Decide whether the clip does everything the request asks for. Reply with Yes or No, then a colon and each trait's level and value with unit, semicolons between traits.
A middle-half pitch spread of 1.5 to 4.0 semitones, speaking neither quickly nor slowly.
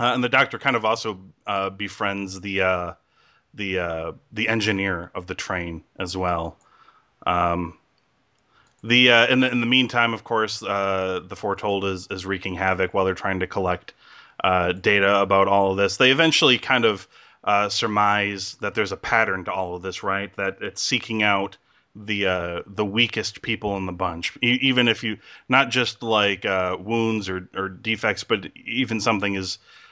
Yes: average, 3.1 semitones; average, 180 wpm